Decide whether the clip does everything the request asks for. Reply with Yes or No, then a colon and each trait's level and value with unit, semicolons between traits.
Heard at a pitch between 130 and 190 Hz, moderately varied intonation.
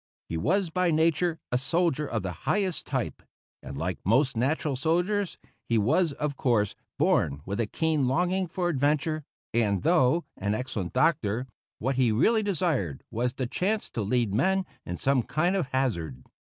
No: low, 135 Hz; wide, 7.3 semitones